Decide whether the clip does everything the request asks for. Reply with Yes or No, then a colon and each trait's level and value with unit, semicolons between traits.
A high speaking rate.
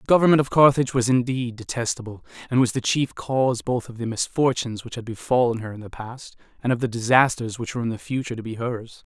Yes: fast, 230 wpm